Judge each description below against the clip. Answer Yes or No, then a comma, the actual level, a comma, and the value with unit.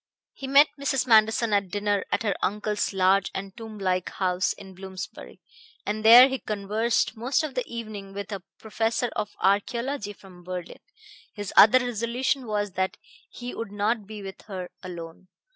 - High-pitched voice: Yes, high, 210 Hz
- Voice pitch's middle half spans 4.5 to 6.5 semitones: No, average, 3.3 semitones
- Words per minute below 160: No, average, 165 wpm